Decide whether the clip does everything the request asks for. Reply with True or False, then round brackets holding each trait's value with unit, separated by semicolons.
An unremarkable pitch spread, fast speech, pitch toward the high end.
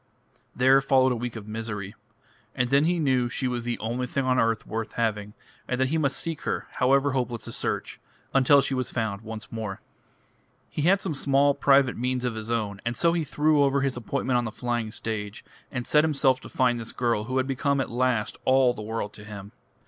False (3.3 semitones; 215 wpm; 125 Hz)